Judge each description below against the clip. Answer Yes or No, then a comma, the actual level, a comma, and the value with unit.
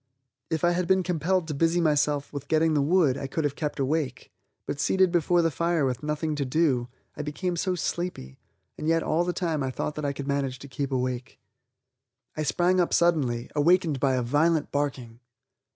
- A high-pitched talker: No, medium, 150 Hz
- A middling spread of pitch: Yes, average, 3.6 semitones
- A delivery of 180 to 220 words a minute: Yes, average, 200 wpm